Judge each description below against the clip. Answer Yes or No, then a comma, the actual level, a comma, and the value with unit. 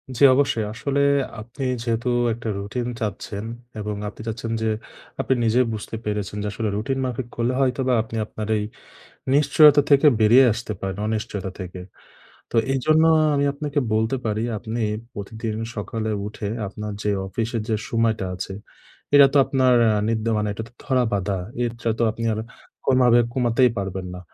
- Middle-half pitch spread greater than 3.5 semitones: No, average, 3.2 semitones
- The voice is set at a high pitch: No, low, 115 Hz